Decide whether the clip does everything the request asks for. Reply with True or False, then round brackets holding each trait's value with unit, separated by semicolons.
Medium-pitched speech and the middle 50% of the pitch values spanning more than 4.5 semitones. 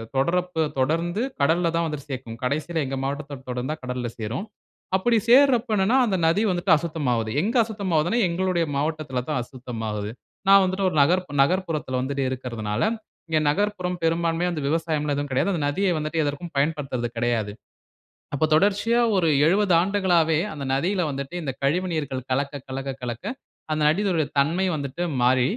True (155 Hz; 5.0 semitones)